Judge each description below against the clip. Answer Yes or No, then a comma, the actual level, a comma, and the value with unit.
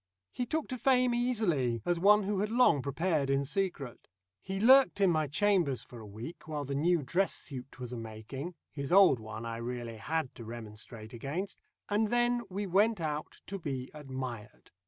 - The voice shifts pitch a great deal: Yes, wide, 8.1 semitones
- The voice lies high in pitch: No, medium, 155 Hz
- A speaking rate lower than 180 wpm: No, average, 185 wpm